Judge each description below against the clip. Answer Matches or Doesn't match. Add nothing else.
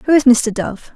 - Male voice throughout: Doesn't match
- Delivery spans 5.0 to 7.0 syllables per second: Doesn't match